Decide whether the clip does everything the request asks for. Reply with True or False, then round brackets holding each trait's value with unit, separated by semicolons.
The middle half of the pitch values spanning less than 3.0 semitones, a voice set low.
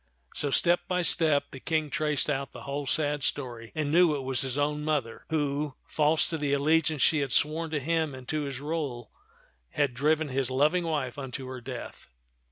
False (2.6 semitones; 145 Hz)